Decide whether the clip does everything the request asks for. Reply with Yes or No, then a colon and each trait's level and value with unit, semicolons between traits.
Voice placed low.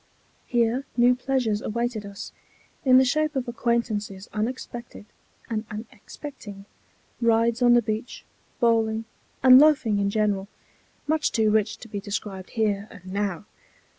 No: high, 225 Hz